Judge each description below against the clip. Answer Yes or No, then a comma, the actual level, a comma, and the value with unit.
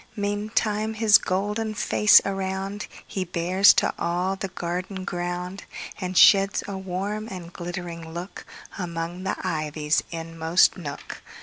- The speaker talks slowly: Yes, slow, 110 wpm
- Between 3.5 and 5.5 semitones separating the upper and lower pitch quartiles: No, average, 2.7 semitones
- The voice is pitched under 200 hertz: Yes, medium, 185 Hz